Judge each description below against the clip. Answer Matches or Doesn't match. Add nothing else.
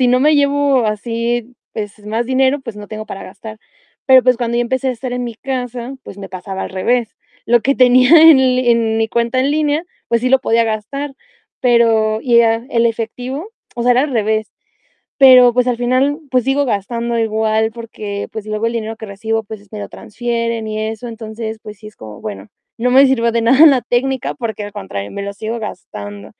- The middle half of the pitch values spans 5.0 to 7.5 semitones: Doesn't match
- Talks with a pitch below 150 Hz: Doesn't match